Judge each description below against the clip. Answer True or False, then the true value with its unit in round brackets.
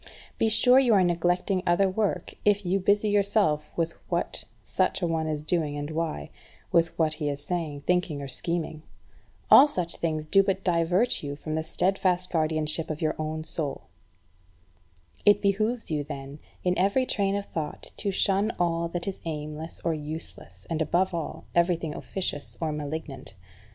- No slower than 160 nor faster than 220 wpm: True (170 wpm)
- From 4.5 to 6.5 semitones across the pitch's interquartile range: False (3.7 semitones)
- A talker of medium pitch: True (170 Hz)